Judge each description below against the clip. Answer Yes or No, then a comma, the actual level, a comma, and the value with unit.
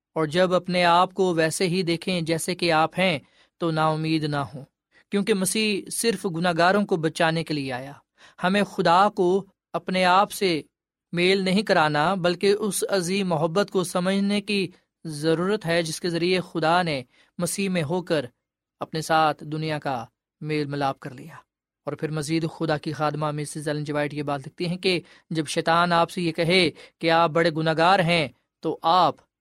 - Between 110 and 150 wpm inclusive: No, average, 180 wpm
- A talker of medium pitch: Yes, medium, 170 Hz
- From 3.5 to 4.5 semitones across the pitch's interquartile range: No, average, 3.0 semitones